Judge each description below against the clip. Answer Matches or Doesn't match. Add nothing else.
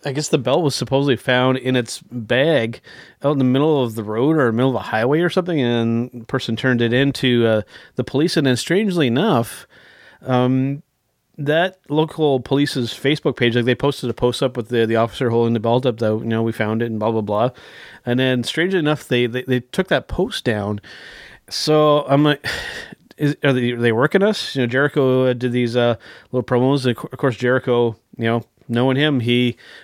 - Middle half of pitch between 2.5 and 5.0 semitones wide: Matches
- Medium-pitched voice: Doesn't match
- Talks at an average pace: Doesn't match